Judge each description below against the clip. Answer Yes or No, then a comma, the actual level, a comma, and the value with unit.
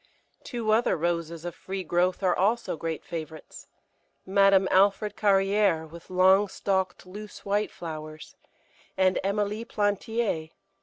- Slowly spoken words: Yes, slow, 120 wpm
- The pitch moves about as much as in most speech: Yes, average, 3.3 semitones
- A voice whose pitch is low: No, high, 190 Hz